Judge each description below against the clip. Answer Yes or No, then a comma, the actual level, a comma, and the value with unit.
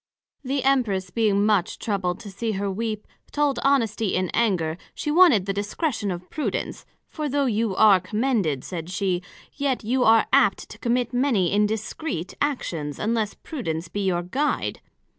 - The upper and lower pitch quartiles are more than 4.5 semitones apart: Yes, average, 5.3 semitones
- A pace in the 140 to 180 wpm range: Yes, average, 160 wpm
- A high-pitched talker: Yes, high, 215 Hz